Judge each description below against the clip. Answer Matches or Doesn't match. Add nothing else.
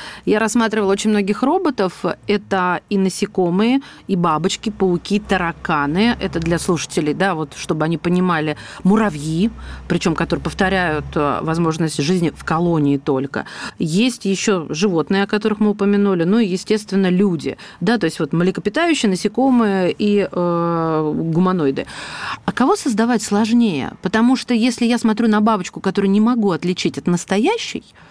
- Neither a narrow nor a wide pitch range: Matches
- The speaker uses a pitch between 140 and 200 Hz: Matches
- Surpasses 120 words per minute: Matches